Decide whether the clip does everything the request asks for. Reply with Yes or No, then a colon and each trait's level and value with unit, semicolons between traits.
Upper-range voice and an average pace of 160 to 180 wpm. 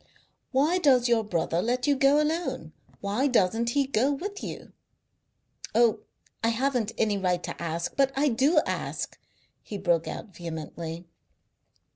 No: high, 235 Hz; average, 145 wpm